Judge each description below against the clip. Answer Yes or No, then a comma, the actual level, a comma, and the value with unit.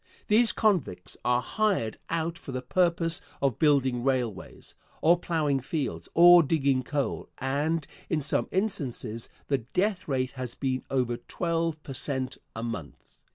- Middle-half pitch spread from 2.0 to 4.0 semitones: No, average, 4.6 semitones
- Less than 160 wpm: Yes, average, 145 wpm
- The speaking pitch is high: No, medium, 140 Hz